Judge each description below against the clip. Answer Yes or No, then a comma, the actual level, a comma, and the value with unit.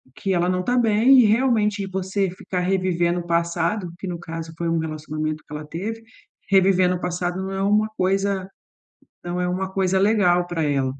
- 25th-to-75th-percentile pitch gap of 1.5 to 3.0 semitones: Yes, narrow, 2.5 semitones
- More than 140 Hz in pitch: Yes, medium, 185 Hz